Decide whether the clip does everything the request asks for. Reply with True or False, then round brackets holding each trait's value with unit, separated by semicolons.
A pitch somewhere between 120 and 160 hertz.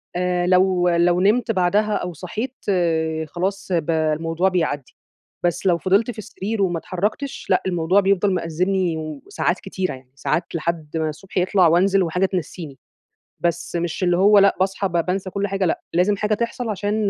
False (180 Hz)